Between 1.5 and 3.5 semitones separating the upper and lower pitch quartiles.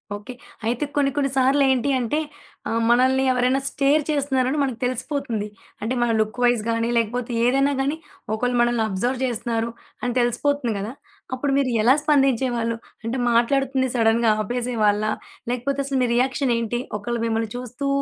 Yes: average, 2.7 semitones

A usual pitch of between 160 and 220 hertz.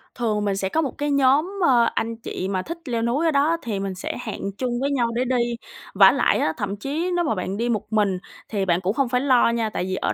No: high, 235 Hz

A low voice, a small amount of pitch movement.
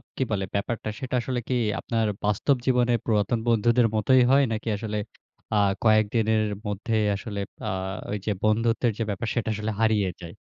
Yes: low, 110 Hz; narrow, 2.0 semitones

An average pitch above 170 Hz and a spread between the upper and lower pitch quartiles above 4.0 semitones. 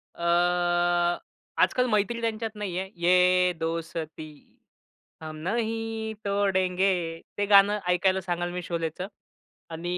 No: high, 190 Hz; average, 3.1 semitones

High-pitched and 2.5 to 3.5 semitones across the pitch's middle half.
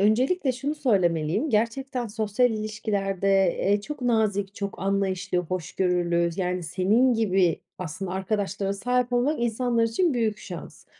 No: high, 205 Hz; average, 4.4 semitones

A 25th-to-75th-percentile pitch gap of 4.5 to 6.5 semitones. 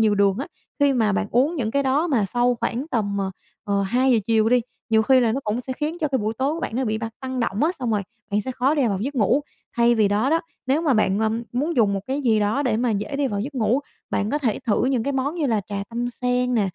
No: average, 3.9 semitones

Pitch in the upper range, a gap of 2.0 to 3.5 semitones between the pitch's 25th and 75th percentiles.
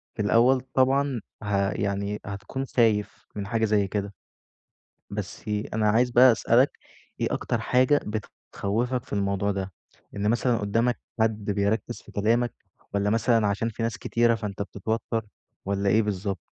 No: low, 110 Hz; average, 2.7 semitones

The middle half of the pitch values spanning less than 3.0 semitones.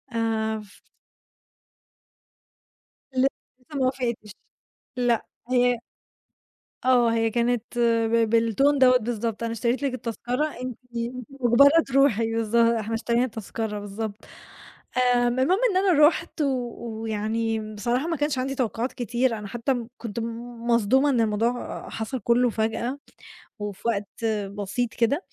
Yes: narrow, 2.5 semitones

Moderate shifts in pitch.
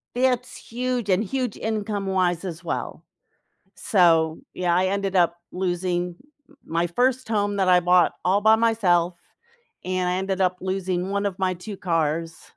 Yes: average, 3.1 semitones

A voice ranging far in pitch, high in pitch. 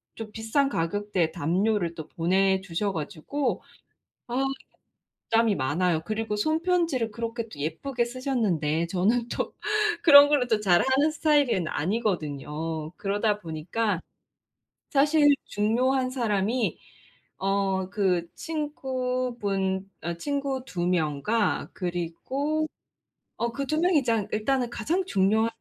Yes: wide, 6.4 semitones; high, 215 Hz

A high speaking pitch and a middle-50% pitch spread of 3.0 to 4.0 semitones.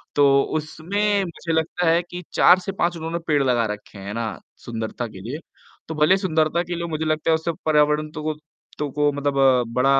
No: medium, 155 Hz; average, 3.7 semitones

